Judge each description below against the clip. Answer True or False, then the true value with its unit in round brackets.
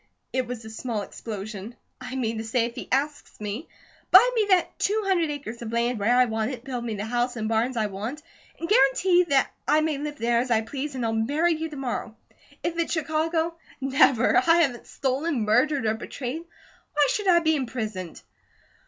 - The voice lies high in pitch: True (255 Hz)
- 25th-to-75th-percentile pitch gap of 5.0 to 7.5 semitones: True (5.6 semitones)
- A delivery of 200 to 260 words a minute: True (205 wpm)